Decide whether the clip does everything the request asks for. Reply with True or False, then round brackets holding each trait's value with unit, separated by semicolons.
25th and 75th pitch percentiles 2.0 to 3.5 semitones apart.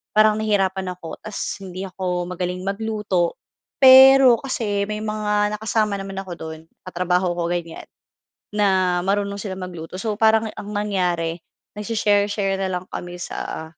True (2.8 semitones)